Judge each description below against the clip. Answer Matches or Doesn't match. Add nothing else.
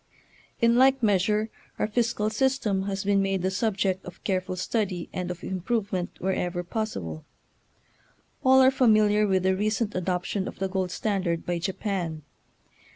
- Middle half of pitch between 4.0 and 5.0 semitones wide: Doesn't match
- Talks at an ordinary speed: Matches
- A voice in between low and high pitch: Doesn't match